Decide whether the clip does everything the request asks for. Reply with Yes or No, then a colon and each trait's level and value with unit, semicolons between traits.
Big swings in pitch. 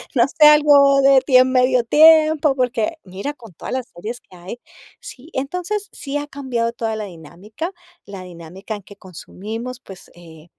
Yes: wide, 6.1 semitones